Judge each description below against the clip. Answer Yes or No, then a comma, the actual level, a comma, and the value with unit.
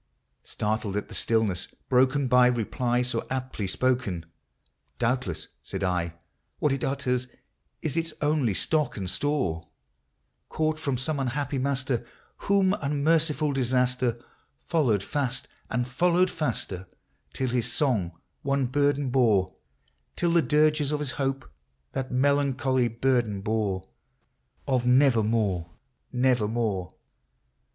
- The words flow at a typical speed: No, slow, 130 wpm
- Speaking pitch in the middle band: No, low, 130 Hz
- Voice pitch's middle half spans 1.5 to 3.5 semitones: No, average, 4.3 semitones